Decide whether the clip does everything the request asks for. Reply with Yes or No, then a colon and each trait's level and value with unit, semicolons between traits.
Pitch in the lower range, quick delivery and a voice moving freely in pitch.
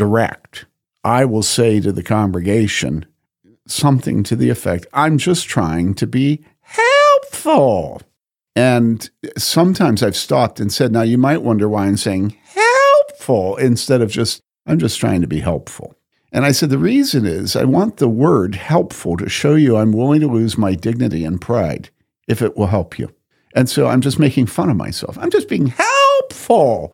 No: low, 120 Hz; average, 175 wpm; wide, 6.2 semitones